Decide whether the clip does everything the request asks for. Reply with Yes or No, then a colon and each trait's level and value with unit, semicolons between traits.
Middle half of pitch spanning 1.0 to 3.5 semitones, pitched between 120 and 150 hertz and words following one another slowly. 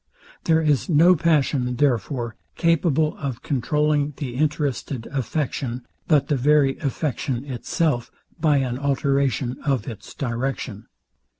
Yes: average, 3.2 semitones; medium, 140 Hz; slow, 115 wpm